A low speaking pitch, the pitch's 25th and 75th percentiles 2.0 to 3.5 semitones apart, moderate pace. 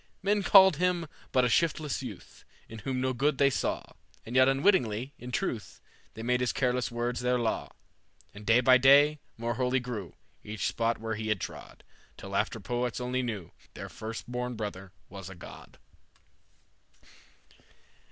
Yes: low, 125 Hz; average, 2.9 semitones; average, 165 wpm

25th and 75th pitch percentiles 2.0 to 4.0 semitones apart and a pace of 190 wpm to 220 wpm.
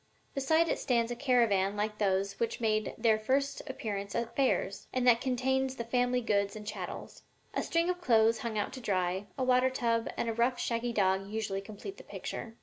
Yes: average, 3.4 semitones; average, 195 wpm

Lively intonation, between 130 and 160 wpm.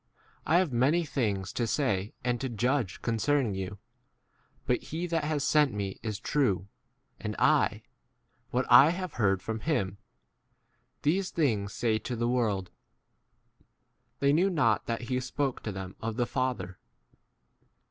Yes: wide, 5.7 semitones; average, 155 wpm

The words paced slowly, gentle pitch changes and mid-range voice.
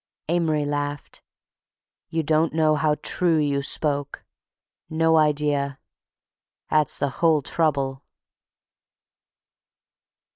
Yes: slow, 85 wpm; narrow, 1.8 semitones; medium, 150 Hz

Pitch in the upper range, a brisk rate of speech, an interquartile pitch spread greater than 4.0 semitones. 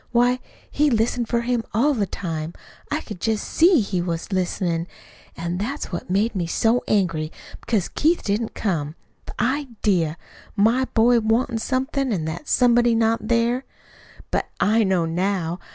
No: high, 220 Hz; average, 155 wpm; average, 5.3 semitones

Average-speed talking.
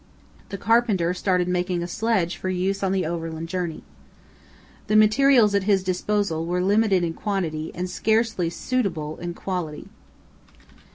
Yes: average, 145 wpm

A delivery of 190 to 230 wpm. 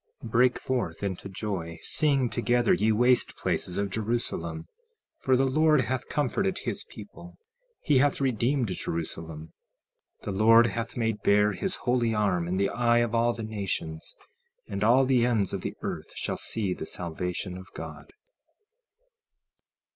No: average, 155 wpm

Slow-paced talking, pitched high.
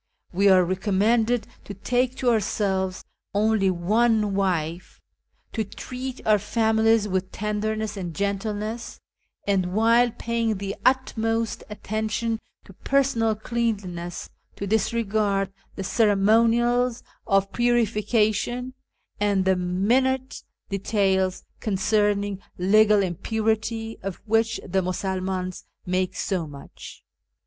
Yes: slow, 105 wpm; high, 210 Hz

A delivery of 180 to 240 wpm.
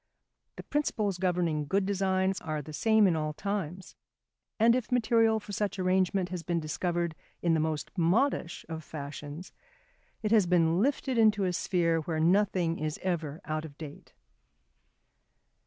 No: average, 155 wpm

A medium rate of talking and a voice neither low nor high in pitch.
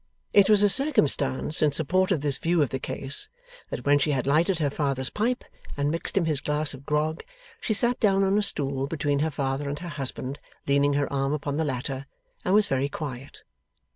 No: fast, 210 wpm; medium, 145 Hz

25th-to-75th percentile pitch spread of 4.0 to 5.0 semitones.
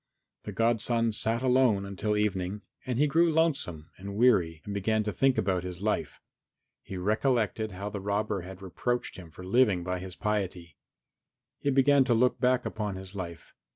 Yes: average, 4.5 semitones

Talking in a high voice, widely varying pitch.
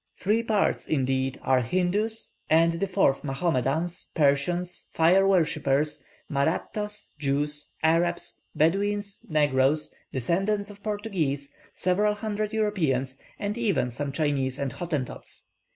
No: medium, 165 Hz; wide, 6.4 semitones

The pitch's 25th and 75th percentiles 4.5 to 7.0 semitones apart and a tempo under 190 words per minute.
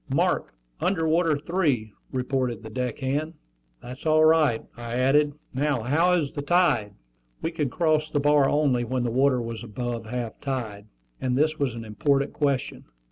No: average, 4.1 semitones; average, 170 wpm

